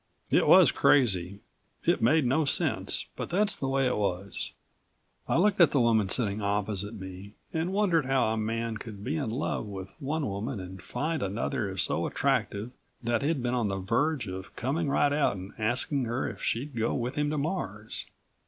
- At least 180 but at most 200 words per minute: Yes, average, 190 wpm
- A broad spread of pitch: Yes, wide, 5.8 semitones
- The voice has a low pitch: Yes, low, 120 Hz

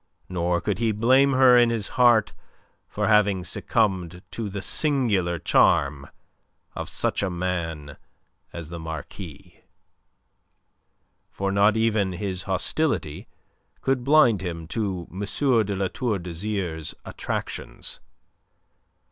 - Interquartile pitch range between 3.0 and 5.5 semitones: Yes, average, 4.6 semitones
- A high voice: No, low, 100 Hz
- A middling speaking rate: No, slow, 115 wpm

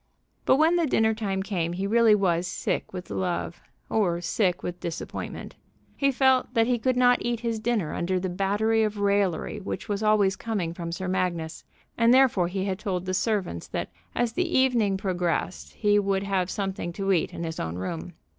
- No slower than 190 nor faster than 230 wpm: Yes, average, 195 wpm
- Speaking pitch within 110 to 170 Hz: No, high, 195 Hz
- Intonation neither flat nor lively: Yes, average, 4.0 semitones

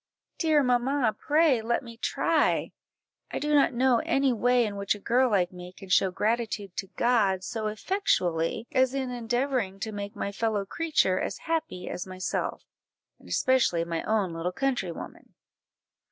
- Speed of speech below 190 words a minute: Yes, average, 160 wpm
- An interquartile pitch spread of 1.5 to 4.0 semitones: No, average, 5.2 semitones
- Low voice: No, high, 225 Hz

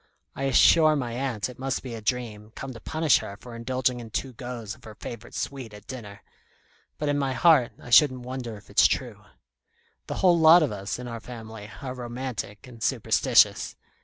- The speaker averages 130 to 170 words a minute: No, average, 195 wpm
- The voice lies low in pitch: Yes, low, 125 Hz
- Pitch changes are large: No, average, 3.0 semitones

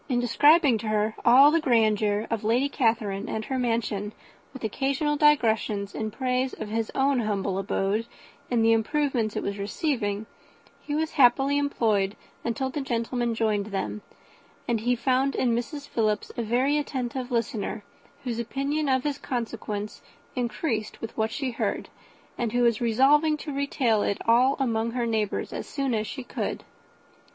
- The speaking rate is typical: Yes, average, 160 wpm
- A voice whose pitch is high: Yes, high, 235 Hz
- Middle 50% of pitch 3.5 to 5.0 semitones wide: Yes, average, 3.8 semitones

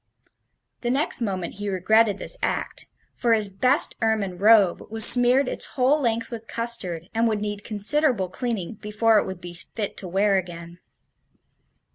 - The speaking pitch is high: Yes, high, 215 Hz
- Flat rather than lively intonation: No, average, 3.5 semitones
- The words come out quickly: No, average, 160 wpm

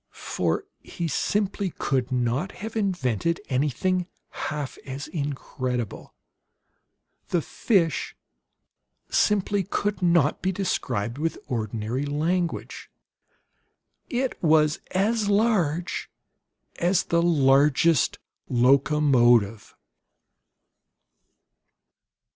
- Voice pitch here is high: No, medium, 155 Hz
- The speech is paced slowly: Yes, slow, 80 wpm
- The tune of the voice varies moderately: No, wide, 6.0 semitones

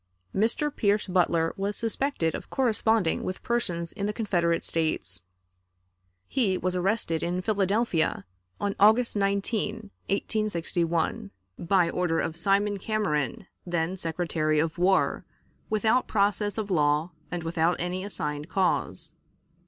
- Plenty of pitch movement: No, average, 4.0 semitones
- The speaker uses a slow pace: Yes, slow, 120 wpm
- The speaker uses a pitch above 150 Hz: Yes, medium, 185 Hz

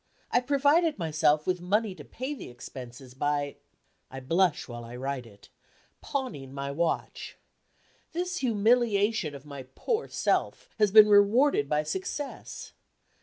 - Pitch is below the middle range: No, medium, 180 Hz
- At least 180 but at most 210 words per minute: No, slow, 135 wpm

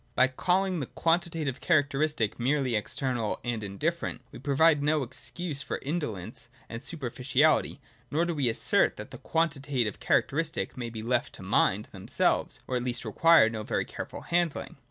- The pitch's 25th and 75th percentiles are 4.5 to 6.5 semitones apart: Yes, average, 5.1 semitones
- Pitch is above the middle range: No, medium, 140 Hz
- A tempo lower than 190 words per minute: Yes, average, 155 wpm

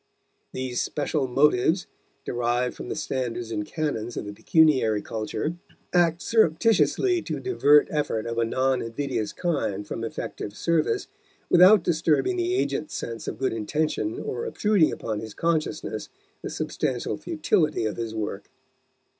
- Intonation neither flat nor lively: No, wide, 6.7 semitones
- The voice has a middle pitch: Yes, medium, 145 Hz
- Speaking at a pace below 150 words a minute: Yes, average, 140 wpm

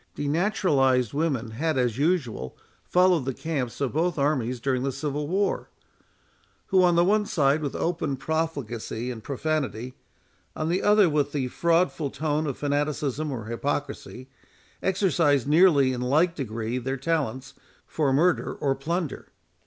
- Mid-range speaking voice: Yes, medium, 145 Hz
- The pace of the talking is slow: No, average, 145 wpm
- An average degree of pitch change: Yes, average, 4.0 semitones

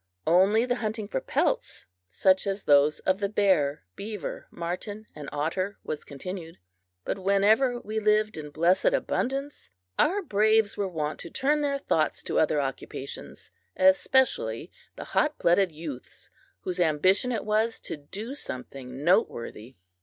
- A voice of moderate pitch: No, high, 195 Hz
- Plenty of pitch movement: Yes, wide, 5.9 semitones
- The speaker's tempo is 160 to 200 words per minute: No, average, 145 wpm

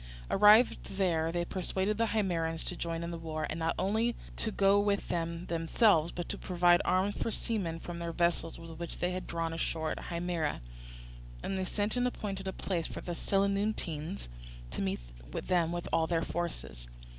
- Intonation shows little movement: No, average, 3.1 semitones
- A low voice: No, medium, 175 Hz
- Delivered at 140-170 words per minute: No, average, 185 wpm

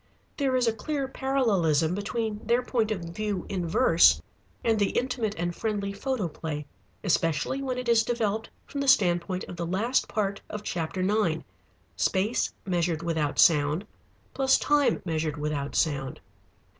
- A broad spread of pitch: Yes, wide, 5.9 semitones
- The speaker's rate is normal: Yes, average, 150 wpm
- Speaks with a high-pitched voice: Yes, high, 200 Hz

